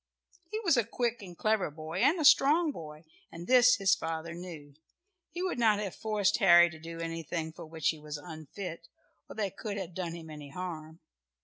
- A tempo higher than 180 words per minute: Yes, average, 200 wpm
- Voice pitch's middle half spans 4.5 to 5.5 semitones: Yes, average, 5.2 semitones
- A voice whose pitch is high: No, medium, 175 Hz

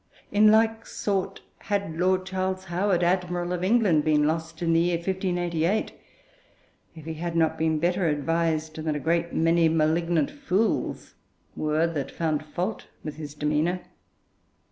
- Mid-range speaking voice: Yes, medium, 170 Hz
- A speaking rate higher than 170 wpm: No, average, 145 wpm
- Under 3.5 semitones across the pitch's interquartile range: Yes, average, 2.8 semitones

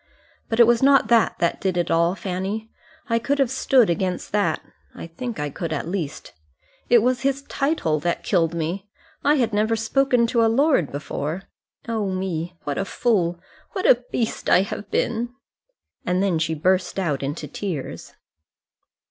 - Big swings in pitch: Yes, wide, 5.8 semitones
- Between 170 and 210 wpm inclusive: Yes, average, 175 wpm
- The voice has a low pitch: No, high, 195 Hz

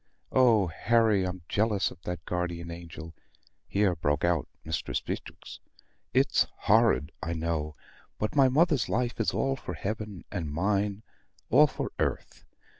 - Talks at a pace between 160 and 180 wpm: No, average, 140 wpm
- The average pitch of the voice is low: Yes, very low, 95 Hz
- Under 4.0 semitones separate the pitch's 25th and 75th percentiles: No, average, 4.8 semitones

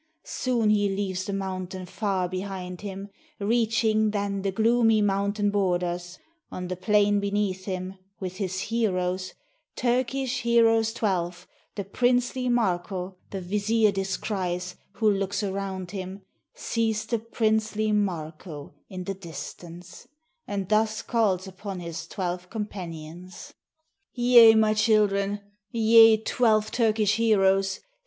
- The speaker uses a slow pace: Yes, slow, 120 wpm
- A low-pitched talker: No, high, 200 Hz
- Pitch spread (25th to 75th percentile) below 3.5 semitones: Yes, average, 2.9 semitones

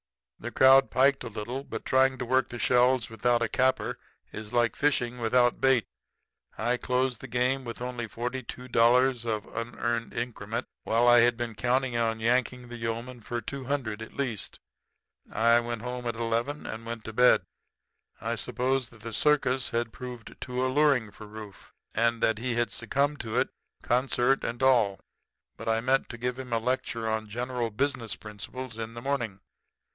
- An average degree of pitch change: No, narrow, 2.0 semitones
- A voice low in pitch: Yes, low, 120 Hz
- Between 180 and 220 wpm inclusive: Yes, average, 185 wpm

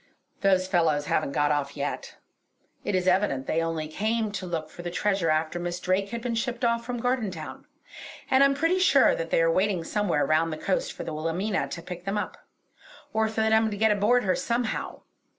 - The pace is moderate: No, fast, 210 wpm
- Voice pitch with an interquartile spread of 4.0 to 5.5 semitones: Yes, average, 5.0 semitones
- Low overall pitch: No, high, 190 Hz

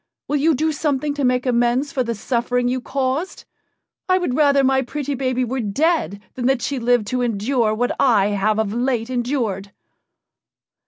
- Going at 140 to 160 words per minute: No, average, 175 wpm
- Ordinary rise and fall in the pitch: Yes, average, 3.0 semitones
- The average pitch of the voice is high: Yes, very high, 250 Hz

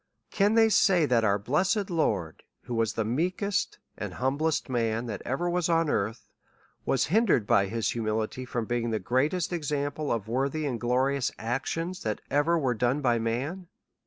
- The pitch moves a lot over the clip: Yes, wide, 6.3 semitones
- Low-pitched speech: Yes, low, 130 Hz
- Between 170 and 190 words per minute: Yes, average, 175 wpm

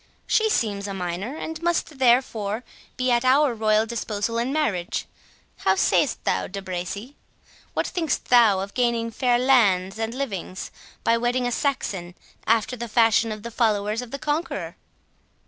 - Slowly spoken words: No, average, 155 wpm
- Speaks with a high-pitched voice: Yes, high, 230 Hz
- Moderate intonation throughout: Yes, average, 3.8 semitones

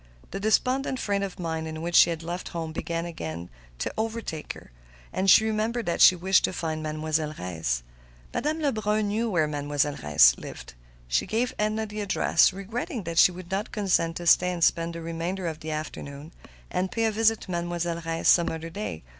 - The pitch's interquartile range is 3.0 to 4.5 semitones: No, average, 4.9 semitones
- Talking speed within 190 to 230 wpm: Yes, average, 195 wpm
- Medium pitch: Yes, medium, 175 Hz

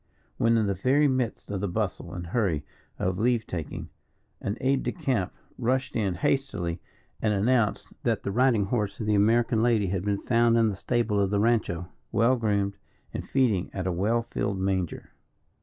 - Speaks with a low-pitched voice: Yes, low, 105 Hz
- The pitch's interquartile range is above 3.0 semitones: Yes, average, 3.4 semitones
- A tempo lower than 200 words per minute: Yes, average, 185 wpm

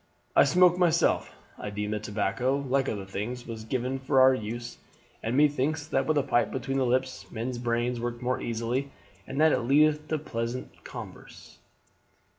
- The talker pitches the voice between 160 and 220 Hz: No, low, 130 Hz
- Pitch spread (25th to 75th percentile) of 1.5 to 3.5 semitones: Yes, average, 3.1 semitones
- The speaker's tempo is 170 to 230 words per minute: Yes, average, 175 wpm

